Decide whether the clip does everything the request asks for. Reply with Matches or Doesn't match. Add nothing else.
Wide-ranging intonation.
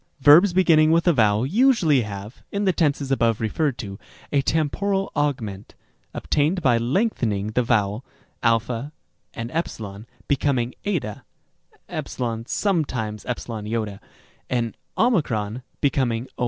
Matches